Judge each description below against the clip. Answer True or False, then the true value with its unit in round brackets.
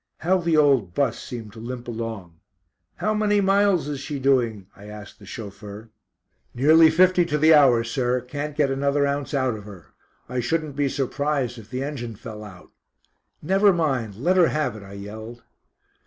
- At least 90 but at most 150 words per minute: False (180 wpm)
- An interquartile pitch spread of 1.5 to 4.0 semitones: False (5.4 semitones)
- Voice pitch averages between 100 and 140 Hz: True (135 Hz)